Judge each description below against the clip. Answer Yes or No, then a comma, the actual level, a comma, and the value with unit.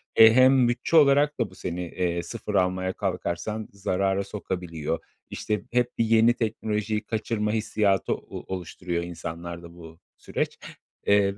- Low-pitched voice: Yes, low, 100 Hz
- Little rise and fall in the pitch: No, average, 4.1 semitones